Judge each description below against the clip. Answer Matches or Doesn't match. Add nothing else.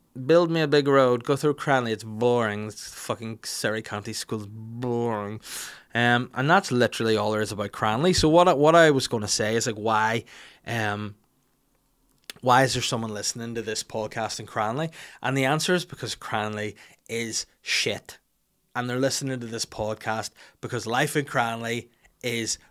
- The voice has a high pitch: Doesn't match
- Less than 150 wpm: Doesn't match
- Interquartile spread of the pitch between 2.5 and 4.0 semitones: Matches